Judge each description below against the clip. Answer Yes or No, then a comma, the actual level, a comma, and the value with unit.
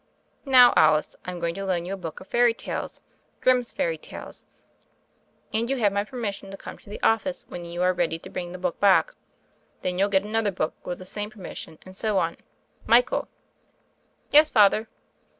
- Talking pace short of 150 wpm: No, average, 195 wpm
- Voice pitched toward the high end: Yes, high, 195 Hz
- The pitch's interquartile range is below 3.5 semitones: No, average, 4.1 semitones